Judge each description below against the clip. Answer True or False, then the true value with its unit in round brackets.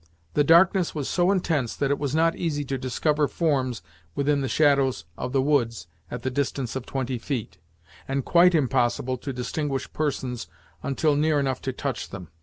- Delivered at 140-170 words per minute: False (180 wpm)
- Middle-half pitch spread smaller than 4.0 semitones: True (2.9 semitones)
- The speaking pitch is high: False (140 Hz)